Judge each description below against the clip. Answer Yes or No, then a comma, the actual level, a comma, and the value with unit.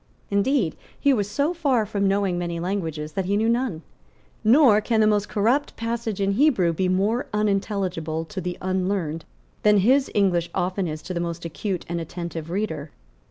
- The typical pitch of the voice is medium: No, high, 195 Hz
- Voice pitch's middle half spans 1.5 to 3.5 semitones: No, average, 4.0 semitones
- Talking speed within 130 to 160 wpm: No, average, 175 wpm